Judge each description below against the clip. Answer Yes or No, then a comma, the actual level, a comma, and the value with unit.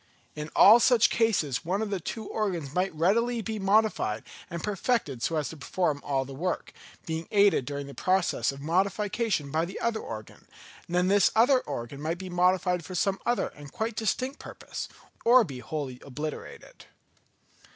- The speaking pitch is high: No, medium, 180 Hz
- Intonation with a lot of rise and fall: Yes, wide, 6.4 semitones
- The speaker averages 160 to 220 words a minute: Yes, average, 175 wpm